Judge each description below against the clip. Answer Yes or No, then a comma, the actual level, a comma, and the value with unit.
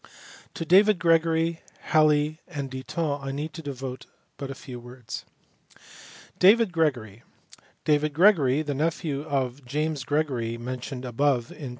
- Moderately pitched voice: Yes, medium, 145 Hz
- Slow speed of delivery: Yes, slow, 130 wpm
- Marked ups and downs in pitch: No, average, 3.7 semitones